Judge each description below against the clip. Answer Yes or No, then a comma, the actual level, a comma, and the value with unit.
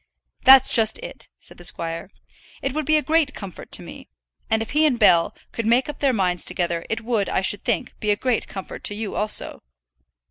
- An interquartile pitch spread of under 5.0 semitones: No, wide, 5.5 semitones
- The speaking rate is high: Yes, fast, 215 wpm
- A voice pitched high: Yes, high, 220 Hz